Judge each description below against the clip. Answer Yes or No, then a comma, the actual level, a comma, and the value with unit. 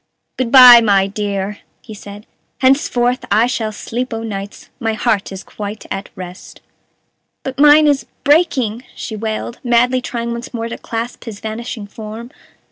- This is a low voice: No, high, 230 Hz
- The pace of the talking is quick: No, average, 155 wpm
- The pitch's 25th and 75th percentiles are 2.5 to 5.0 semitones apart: Yes, average, 3.1 semitones